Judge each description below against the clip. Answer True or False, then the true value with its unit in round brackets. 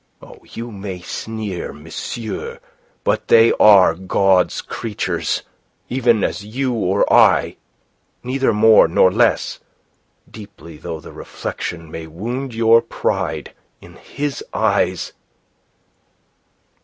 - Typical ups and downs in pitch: True (4.1 semitones)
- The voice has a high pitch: False (110 Hz)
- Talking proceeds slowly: True (105 wpm)